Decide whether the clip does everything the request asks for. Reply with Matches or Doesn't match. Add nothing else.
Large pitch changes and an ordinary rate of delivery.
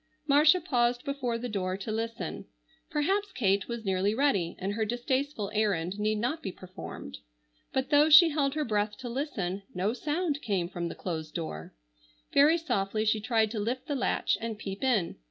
Matches